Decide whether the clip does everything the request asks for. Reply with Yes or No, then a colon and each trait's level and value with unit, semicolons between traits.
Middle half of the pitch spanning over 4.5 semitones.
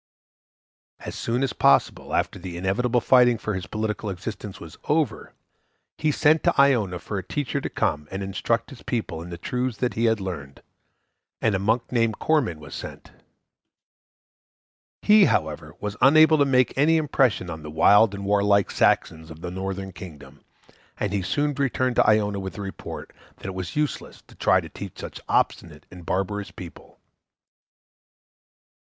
Yes: average, 5.2 semitones